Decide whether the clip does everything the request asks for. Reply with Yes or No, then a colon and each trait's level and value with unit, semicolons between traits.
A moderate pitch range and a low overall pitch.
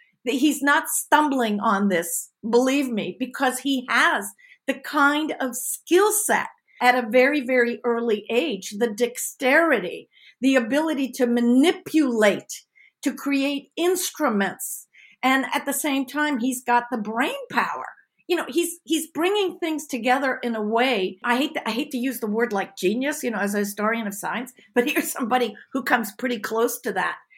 No: average, 3.7 semitones; very high, 255 Hz